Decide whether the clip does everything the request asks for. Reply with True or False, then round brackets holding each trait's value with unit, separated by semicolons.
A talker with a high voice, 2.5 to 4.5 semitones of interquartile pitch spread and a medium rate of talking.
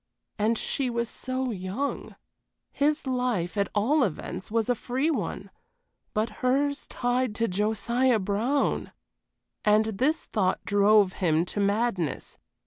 False (225 Hz; 4.1 semitones; 130 wpm)